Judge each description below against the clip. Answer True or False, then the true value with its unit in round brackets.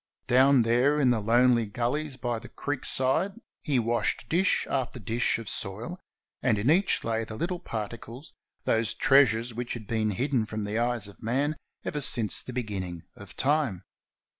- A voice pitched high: False (120 Hz)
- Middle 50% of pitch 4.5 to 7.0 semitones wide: False (3.6 semitones)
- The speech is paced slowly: False (170 wpm)